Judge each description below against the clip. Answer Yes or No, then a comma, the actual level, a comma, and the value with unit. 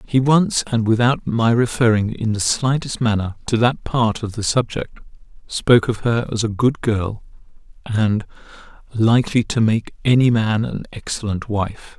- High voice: No, low, 115 Hz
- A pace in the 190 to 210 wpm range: No, average, 160 wpm